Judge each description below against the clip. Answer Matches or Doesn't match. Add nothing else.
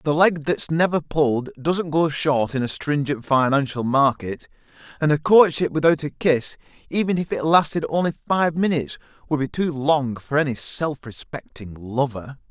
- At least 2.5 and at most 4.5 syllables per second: Doesn't match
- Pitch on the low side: Doesn't match